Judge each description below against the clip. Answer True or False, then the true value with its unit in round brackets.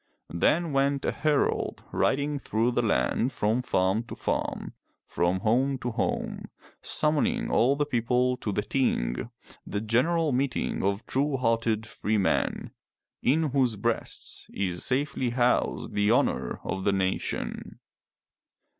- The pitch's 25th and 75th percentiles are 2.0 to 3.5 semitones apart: False (4.7 semitones)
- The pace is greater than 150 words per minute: False (135 wpm)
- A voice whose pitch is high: False (120 Hz)